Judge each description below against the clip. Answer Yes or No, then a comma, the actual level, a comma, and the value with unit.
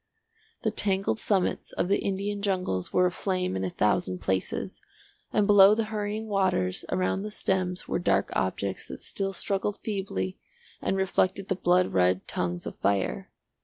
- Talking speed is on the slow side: No, average, 160 wpm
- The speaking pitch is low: No, medium, 185 Hz